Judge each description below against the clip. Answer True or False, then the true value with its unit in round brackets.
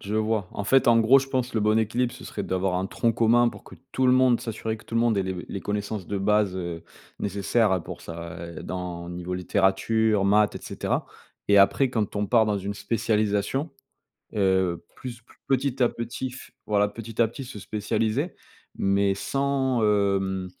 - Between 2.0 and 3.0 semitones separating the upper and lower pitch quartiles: False (3.4 semitones)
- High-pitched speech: False (105 Hz)